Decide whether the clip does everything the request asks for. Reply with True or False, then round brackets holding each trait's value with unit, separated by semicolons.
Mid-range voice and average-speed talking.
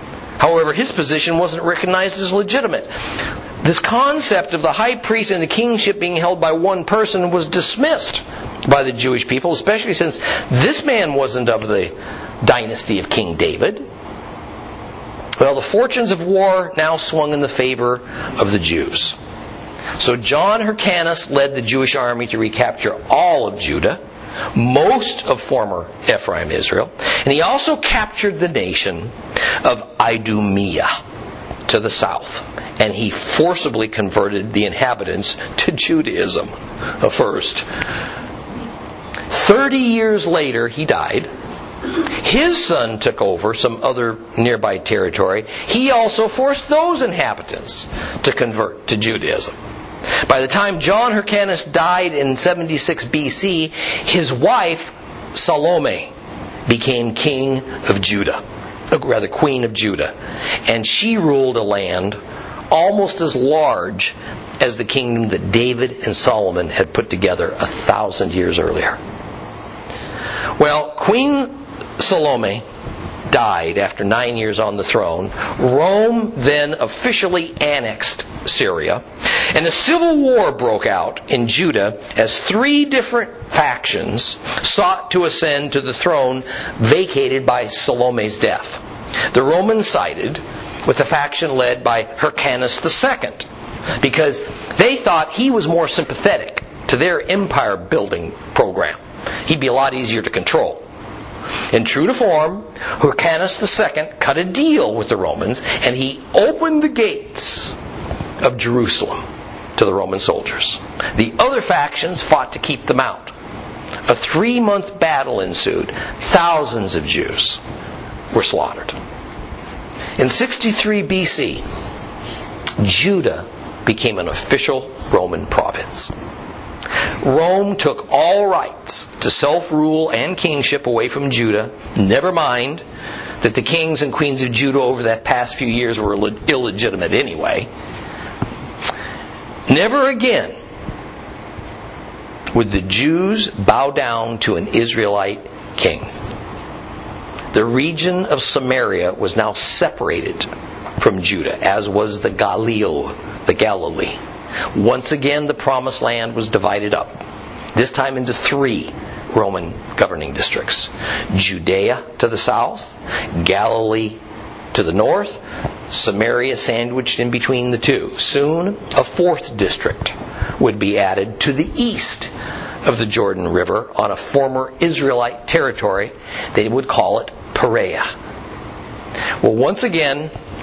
False (155 Hz; 125 wpm)